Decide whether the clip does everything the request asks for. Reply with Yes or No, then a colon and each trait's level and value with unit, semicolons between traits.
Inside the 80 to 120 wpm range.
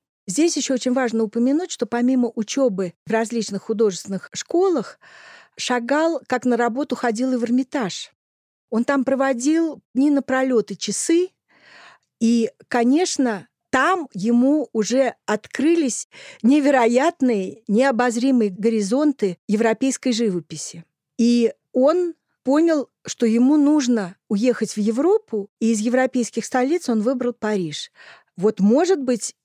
Yes: average, 115 wpm